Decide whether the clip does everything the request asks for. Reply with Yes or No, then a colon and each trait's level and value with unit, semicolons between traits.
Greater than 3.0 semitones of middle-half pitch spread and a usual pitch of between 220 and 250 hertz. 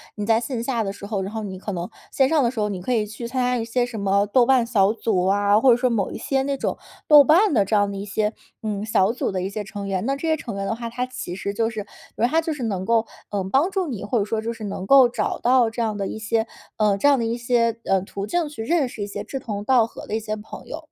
Yes: average, 3.6 semitones; high, 225 Hz